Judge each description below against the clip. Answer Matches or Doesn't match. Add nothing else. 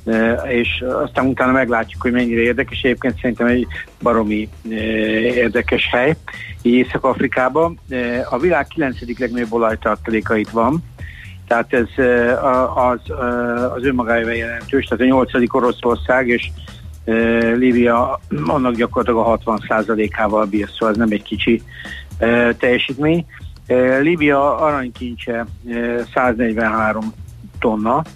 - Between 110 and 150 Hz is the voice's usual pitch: Matches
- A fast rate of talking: Doesn't match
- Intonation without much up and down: Matches